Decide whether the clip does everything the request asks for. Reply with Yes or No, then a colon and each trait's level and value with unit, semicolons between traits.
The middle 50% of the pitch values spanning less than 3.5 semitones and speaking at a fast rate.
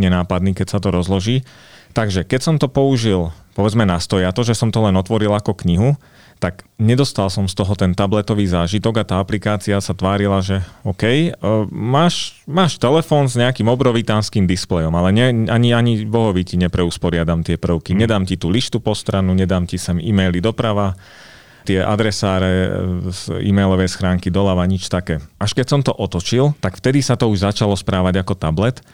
No: average, 3.8 semitones; fast, 175 wpm